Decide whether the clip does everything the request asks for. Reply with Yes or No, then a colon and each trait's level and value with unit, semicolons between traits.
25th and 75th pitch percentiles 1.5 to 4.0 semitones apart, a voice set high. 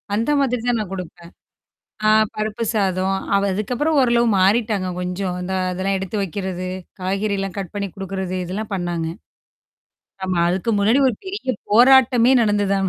Yes: average, 3.6 semitones; high, 195 Hz